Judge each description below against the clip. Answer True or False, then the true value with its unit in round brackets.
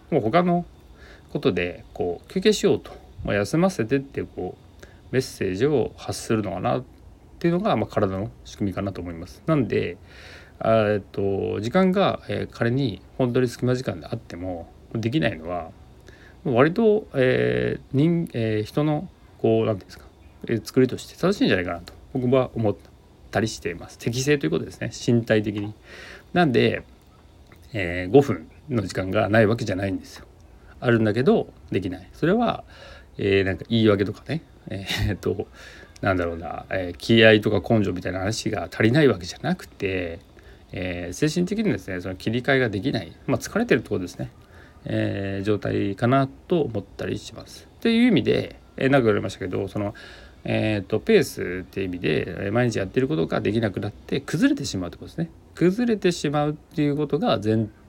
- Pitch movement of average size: False (5.8 semitones)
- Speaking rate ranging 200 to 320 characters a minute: True (315 characters per minute)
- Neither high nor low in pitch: False (110 Hz)